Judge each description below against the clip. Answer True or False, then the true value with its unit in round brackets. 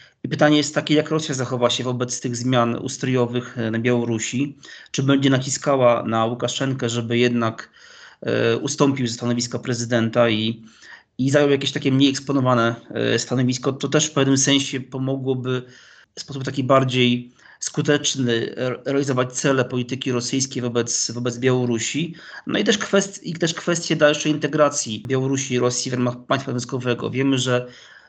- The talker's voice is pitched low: True (130 Hz)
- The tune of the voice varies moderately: False (2.3 semitones)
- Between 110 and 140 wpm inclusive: False (150 wpm)